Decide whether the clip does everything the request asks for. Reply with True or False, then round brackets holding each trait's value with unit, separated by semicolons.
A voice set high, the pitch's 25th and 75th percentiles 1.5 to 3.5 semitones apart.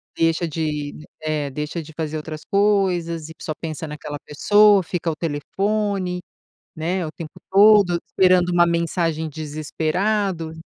False (165 Hz; 3.1 semitones)